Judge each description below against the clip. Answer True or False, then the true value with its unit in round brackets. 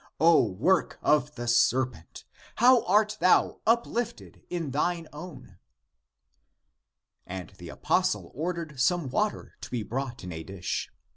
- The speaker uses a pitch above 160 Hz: False (150 Hz)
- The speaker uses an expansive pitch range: True (7.0 semitones)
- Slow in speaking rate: True (130 wpm)